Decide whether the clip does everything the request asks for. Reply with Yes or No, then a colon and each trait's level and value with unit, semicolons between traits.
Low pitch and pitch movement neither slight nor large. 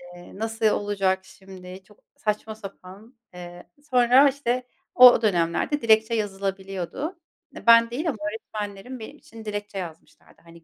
No: high, 210 Hz; average, 3.4 semitones